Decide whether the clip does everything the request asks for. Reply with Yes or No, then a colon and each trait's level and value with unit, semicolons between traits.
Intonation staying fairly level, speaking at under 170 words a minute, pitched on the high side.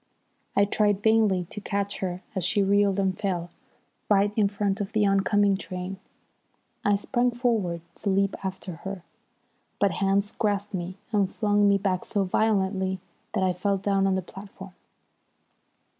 Yes: narrow, 1.4 semitones; average, 160 wpm; high, 195 Hz